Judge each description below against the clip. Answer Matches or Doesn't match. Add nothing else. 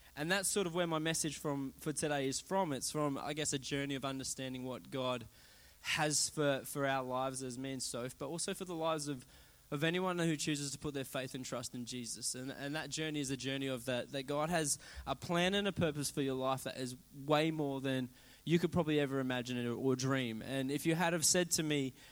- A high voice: Doesn't match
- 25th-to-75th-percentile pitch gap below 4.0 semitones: Matches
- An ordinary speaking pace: Doesn't match